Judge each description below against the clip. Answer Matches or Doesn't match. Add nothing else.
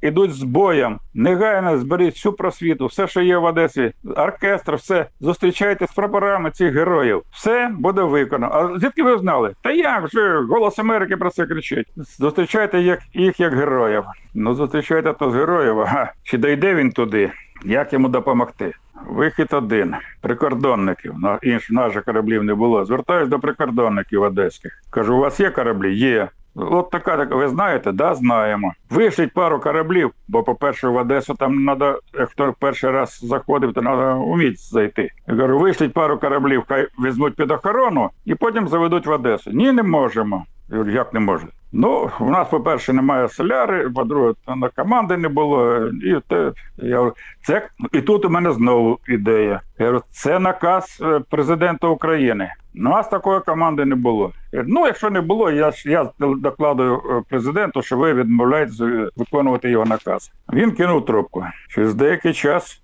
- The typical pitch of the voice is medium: Matches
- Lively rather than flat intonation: Matches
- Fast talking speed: Matches